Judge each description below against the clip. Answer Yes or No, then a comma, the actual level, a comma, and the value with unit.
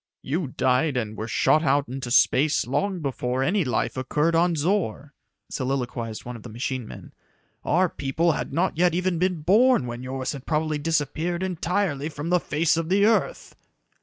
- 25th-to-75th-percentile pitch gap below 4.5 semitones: No, average, 5.1 semitones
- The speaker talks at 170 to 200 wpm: Yes, average, 175 wpm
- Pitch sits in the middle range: Yes, medium, 150 Hz